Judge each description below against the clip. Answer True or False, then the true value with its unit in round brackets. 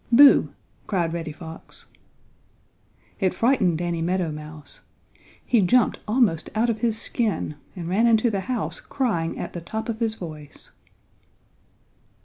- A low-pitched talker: False (190 Hz)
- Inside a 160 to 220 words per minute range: False (135 wpm)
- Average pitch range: False (5.7 semitones)